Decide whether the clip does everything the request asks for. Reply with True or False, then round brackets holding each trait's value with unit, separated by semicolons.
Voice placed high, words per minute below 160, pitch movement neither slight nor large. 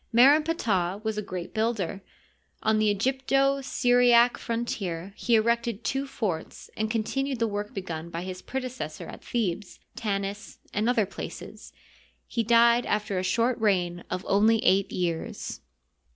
True (220 Hz; 150 wpm; 3.9 semitones)